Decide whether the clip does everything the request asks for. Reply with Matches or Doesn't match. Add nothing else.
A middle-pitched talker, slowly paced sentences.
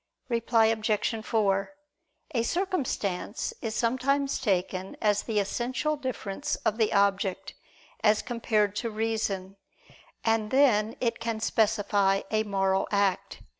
Doesn't match